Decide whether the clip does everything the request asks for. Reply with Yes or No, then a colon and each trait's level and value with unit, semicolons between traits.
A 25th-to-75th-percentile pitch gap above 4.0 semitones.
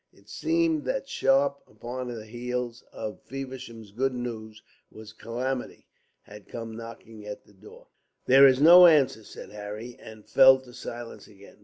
No: average, 3.4 semitones